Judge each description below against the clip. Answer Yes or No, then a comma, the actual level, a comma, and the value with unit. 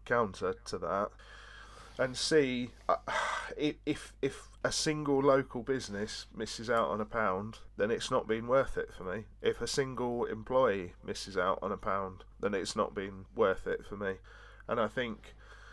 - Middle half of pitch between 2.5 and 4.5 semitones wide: No, average, 5.1 semitones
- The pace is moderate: Yes, average, 170 wpm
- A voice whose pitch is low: Yes, low, 120 Hz